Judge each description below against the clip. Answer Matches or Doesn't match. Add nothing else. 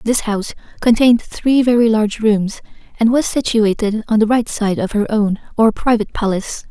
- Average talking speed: Matches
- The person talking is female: Matches